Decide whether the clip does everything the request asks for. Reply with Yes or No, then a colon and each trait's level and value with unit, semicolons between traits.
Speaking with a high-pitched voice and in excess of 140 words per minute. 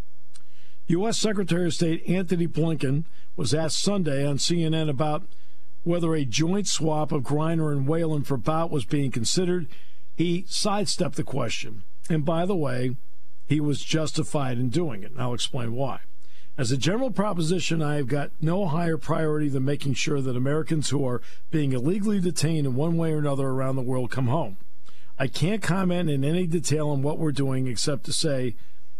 No: medium, 150 Hz; average, 180 wpm